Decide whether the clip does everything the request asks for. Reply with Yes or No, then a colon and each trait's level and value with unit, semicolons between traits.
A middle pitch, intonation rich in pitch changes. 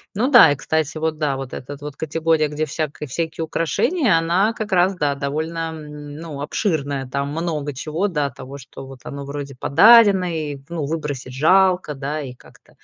No: medium, 155 Hz; average, 2.9 semitones